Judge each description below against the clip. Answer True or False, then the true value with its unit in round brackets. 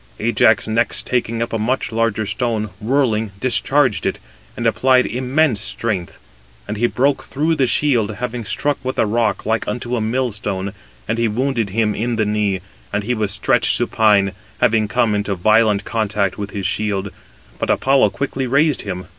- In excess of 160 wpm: True (170 wpm)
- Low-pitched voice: True (110 Hz)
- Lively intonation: False (3.3 semitones)